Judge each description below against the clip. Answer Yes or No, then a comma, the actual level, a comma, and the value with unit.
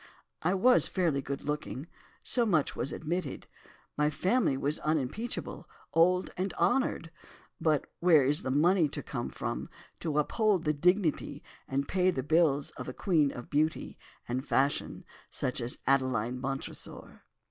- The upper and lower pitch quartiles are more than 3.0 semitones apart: Yes, average, 4.8 semitones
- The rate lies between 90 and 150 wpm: Yes, average, 140 wpm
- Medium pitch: Yes, medium, 150 Hz